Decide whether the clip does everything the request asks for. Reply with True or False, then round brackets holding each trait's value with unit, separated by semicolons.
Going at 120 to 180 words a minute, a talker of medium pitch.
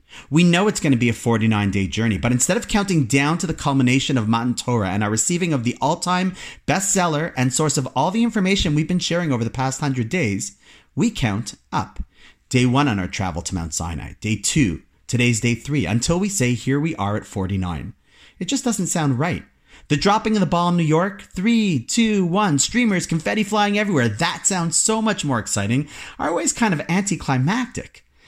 False (205 wpm; 145 Hz)